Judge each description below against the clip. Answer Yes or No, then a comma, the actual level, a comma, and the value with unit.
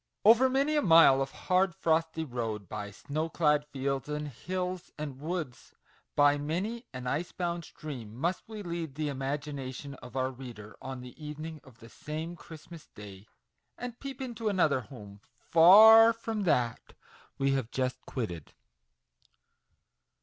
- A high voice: No, medium, 150 Hz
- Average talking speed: Yes, average, 150 wpm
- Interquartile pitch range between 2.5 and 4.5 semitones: No, average, 5.3 semitones